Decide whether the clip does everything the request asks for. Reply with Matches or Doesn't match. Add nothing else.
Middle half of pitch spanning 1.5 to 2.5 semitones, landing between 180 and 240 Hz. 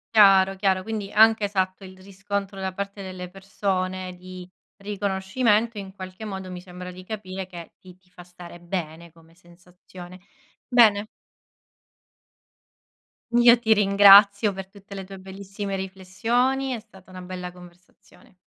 Matches